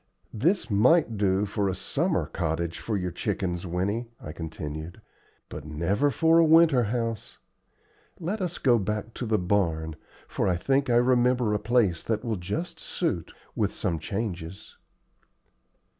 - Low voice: Yes, low, 105 Hz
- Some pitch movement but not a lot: No, wide, 6.1 semitones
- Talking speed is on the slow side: No, average, 150 wpm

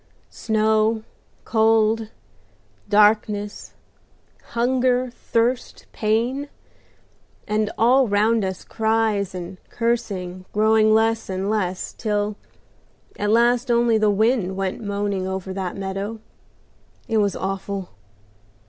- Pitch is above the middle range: Yes, high, 215 Hz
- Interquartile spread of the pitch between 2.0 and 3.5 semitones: Yes, narrow, 2.4 semitones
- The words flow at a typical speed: No, slow, 100 wpm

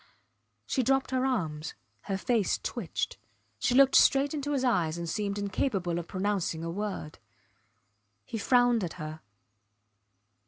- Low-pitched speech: No, high, 205 Hz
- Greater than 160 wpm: No, average, 140 wpm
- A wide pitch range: Yes, wide, 6.9 semitones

